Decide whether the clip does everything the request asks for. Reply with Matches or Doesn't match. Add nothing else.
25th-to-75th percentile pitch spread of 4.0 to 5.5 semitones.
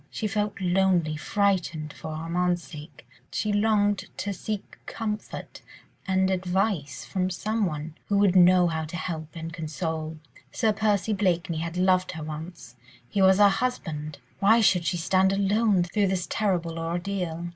Doesn't match